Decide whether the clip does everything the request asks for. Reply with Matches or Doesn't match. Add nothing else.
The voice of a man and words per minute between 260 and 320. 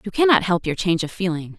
Doesn't match